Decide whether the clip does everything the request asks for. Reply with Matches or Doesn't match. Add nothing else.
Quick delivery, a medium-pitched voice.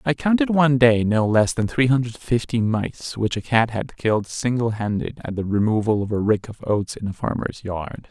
Doesn't match